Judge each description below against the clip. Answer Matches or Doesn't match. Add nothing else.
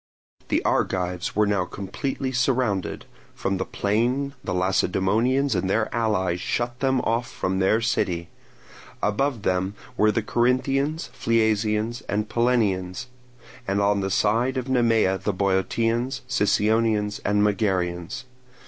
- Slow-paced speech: Matches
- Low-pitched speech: Matches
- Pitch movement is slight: Doesn't match